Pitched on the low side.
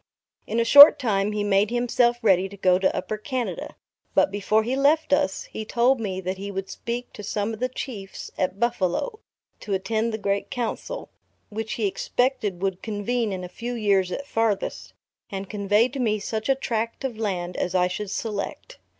No: high, 215 Hz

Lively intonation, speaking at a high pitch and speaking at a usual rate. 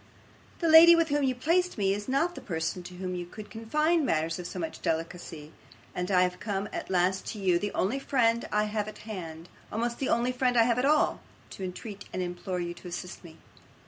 No: wide, 5.9 semitones; high, 205 Hz; fast, 225 wpm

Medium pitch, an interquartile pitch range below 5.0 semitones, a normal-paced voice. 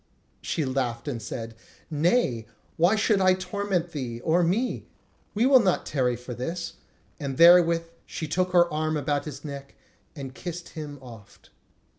No: medium, 155 Hz; average, 5.3 semitones; average, 150 wpm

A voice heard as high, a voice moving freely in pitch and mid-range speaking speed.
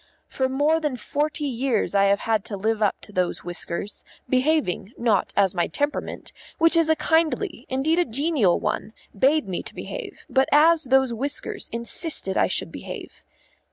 Yes: very high, 265 Hz; wide, 6.7 semitones; average, 170 wpm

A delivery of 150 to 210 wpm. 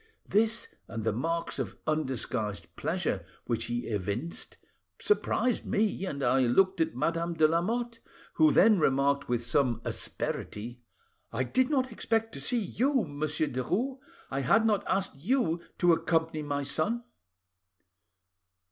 No: average, 140 wpm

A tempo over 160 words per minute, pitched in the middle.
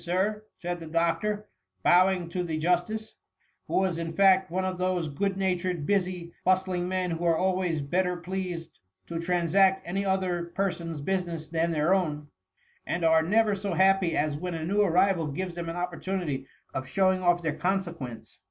Yes: average, 180 wpm; medium, 180 Hz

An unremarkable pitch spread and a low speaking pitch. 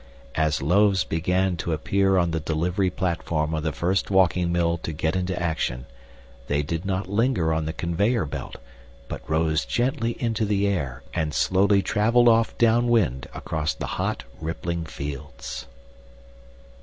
Yes: average, 4.0 semitones; very low, 85 Hz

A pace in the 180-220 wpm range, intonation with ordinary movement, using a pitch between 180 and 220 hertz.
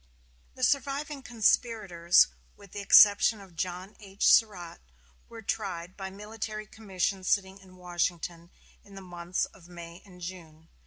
No: average, 140 wpm; average, 3.3 semitones; high, 190 Hz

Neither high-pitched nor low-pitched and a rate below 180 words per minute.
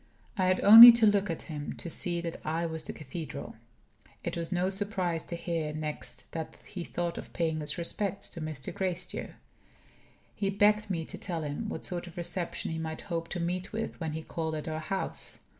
No: medium, 170 Hz; fast, 205 wpm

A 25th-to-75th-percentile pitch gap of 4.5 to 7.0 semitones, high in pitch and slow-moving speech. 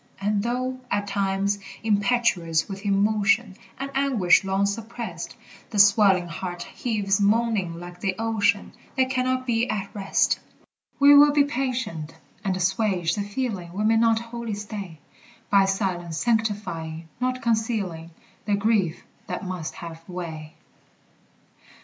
No: average, 3.7 semitones; high, 205 Hz; slow, 130 wpm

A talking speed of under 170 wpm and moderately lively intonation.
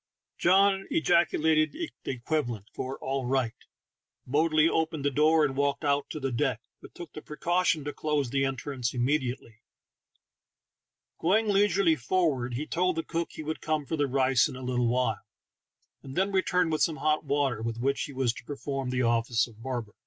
No: average, 180 wpm; average, 4.0 semitones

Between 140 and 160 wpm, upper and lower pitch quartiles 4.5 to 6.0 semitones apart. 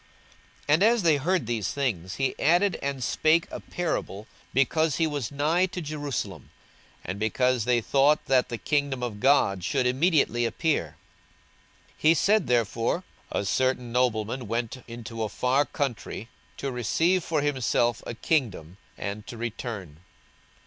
Yes: average, 150 wpm; average, 4.9 semitones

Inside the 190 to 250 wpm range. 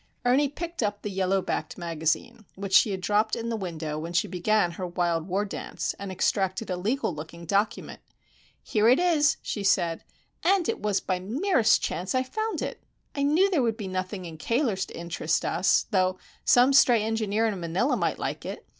Yes: average, 200 wpm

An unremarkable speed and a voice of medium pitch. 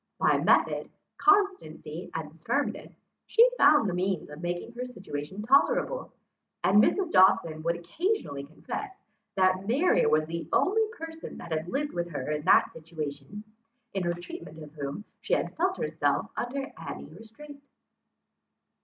No: average, 145 wpm; high, 195 Hz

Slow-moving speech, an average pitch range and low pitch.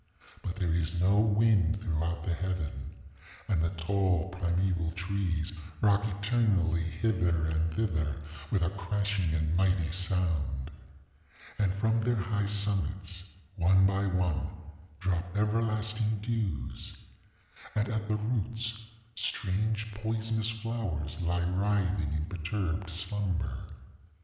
Yes: slow, 115 wpm; average, 3.6 semitones; very low, 95 Hz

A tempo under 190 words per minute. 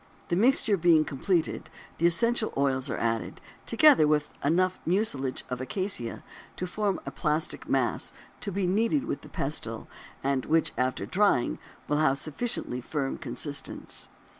Yes: average, 150 wpm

